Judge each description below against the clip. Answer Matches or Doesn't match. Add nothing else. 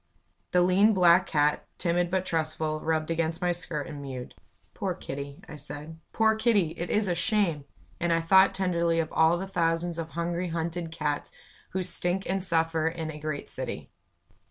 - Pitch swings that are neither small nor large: Doesn't match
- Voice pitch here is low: Doesn't match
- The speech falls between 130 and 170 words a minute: Doesn't match